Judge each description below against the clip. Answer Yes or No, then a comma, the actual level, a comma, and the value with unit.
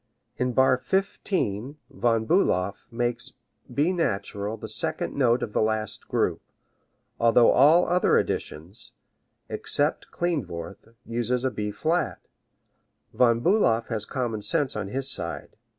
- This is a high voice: No, low, 120 Hz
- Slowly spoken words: Yes, slow, 125 wpm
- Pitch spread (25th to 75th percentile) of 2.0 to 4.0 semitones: No, average, 4.6 semitones